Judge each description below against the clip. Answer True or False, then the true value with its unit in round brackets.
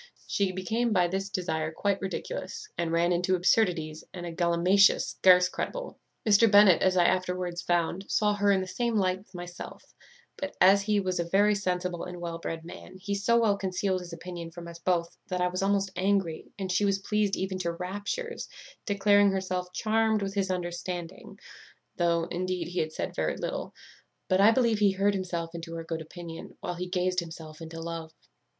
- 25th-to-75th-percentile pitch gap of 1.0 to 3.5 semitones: True (2.6 semitones)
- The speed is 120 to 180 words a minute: False (190 wpm)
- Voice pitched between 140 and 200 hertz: True (185 Hz)